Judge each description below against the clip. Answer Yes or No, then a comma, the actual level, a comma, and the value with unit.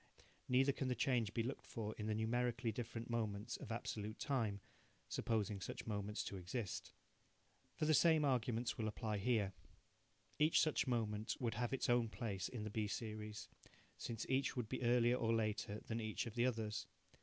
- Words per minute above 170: Yes, average, 180 wpm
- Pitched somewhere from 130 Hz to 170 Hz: No, low, 115 Hz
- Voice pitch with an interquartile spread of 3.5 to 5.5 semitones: No, narrow, 2.4 semitones